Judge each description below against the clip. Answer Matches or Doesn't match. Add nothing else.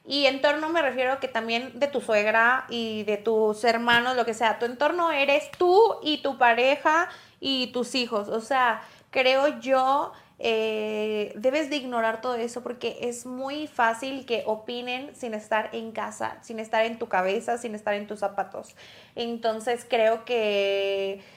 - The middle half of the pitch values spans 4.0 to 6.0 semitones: Doesn't match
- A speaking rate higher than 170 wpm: Doesn't match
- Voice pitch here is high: Matches